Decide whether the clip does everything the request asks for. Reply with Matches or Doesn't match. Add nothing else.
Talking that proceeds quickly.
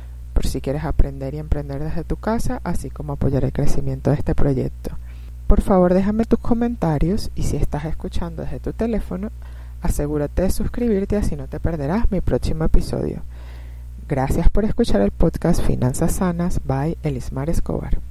Doesn't match